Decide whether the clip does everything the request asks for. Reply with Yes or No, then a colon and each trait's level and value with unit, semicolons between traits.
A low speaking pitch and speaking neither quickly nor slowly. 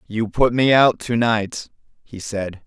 Yes: low, 110 Hz; average, 180 wpm